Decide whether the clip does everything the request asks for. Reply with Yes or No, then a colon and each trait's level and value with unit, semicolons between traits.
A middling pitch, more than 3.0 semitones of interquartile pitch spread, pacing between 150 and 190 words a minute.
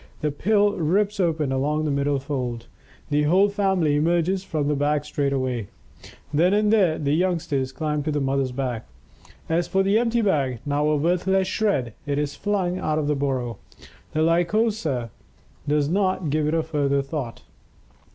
Yes: medium, 150 Hz; average, 4.8 semitones; average, 170 wpm